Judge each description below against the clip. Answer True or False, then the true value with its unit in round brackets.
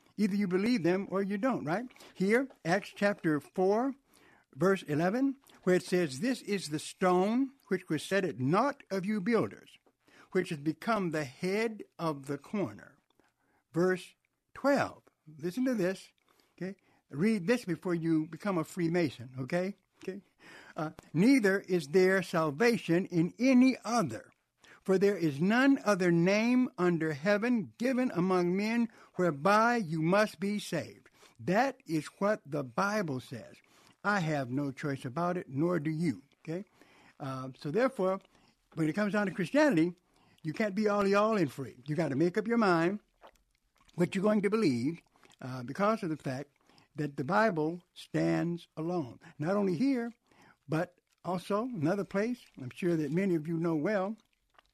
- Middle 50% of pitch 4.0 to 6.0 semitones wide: True (4.7 semitones)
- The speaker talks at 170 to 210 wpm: False (160 wpm)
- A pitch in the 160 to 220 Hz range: True (185 Hz)